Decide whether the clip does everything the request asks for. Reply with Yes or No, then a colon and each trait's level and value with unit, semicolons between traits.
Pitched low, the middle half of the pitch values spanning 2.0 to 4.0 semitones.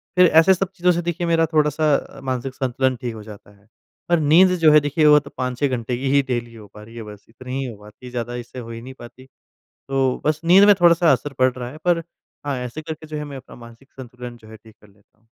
No: low, 130 Hz; average, 4.4 semitones